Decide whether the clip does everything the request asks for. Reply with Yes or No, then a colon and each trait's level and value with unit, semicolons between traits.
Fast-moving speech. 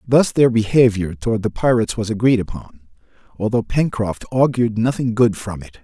No: average, 165 wpm